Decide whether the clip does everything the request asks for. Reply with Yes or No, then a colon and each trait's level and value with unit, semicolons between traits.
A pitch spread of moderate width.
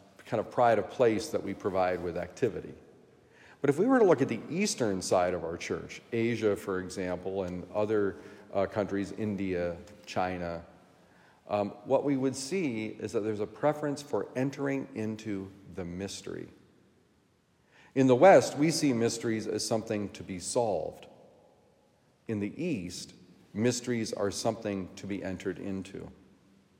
Yes: average, 3.8 semitones